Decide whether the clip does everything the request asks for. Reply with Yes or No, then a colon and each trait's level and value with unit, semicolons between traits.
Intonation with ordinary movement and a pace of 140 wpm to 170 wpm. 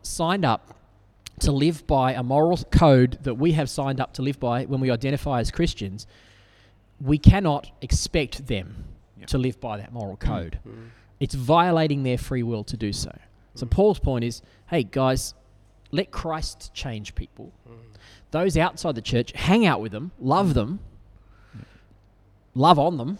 No: wide, 5.7 semitones; average, 160 wpm